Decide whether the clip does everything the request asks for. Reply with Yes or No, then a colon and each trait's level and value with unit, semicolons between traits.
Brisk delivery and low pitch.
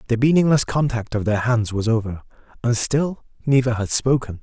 No: average, 175 wpm; low, 120 Hz